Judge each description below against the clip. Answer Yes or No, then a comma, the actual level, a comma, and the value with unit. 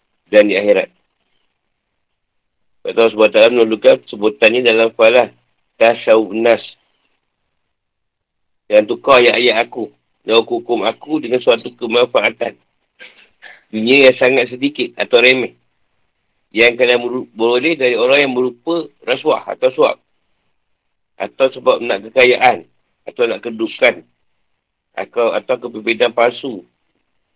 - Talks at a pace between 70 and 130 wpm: Yes, average, 115 wpm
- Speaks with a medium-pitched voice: No, low, 125 Hz